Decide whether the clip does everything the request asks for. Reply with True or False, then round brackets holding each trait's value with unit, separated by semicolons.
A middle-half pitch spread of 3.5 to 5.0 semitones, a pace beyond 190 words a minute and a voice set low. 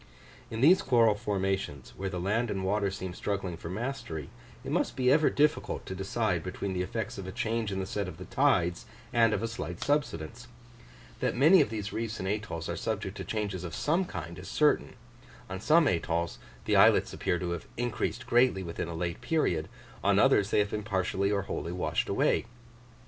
True (4.2 semitones; 200 wpm; 100 Hz)